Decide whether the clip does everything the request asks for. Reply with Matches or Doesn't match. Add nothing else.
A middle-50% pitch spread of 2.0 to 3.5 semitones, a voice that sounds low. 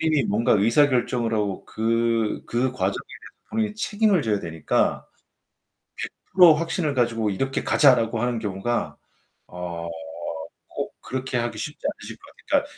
Doesn't match